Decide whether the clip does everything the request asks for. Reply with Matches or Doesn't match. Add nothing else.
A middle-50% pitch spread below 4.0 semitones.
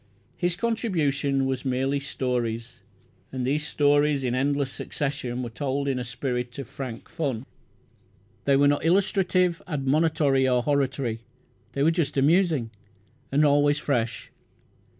Matches